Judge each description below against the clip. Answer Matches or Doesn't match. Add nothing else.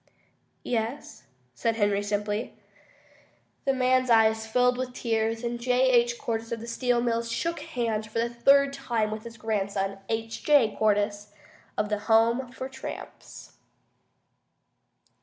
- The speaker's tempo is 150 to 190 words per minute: Doesn't match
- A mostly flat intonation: Matches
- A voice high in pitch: Matches